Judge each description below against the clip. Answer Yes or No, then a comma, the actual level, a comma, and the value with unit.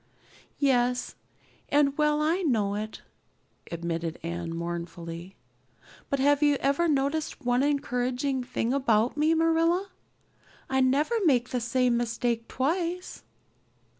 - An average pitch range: Yes, average, 4.7 semitones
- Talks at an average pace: No, slow, 115 wpm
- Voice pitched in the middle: No, very high, 260 Hz